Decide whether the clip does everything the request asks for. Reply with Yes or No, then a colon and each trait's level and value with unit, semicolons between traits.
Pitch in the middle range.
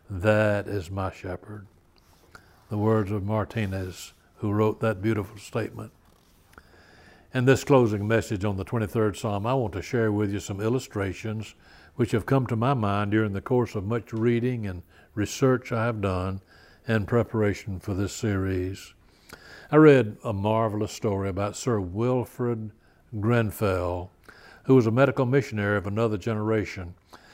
No: low, 105 Hz